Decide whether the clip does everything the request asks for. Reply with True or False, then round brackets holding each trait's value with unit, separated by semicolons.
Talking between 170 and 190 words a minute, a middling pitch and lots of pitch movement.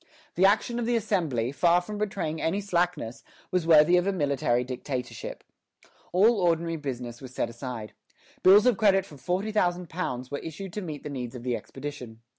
True (175 wpm; 165 Hz; 7.0 semitones)